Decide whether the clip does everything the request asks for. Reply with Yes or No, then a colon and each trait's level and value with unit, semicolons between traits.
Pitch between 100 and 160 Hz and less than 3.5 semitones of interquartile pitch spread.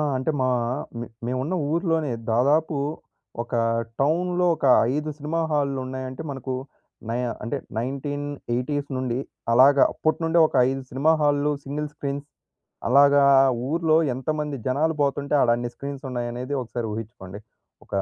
Yes: medium, 140 Hz; average, 2.9 semitones